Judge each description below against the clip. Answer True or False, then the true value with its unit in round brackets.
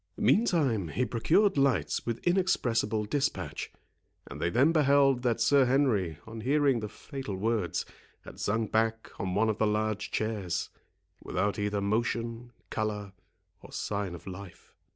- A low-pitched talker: True (115 Hz)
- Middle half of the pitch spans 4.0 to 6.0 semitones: True (4.6 semitones)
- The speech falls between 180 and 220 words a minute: False (145 wpm)